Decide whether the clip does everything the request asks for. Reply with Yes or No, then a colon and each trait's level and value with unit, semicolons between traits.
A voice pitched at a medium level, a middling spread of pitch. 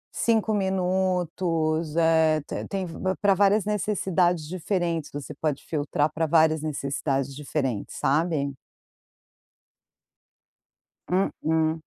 Yes: medium, 160 Hz; average, 3.5 semitones